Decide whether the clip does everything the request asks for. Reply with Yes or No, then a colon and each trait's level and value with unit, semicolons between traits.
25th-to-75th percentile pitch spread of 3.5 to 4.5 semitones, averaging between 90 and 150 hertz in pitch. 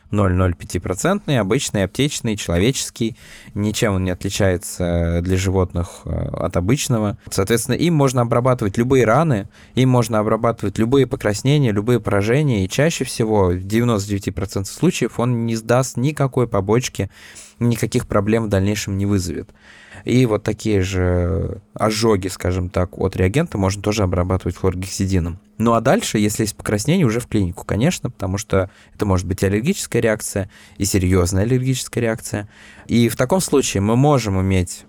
Yes: average, 4.0 semitones; low, 105 Hz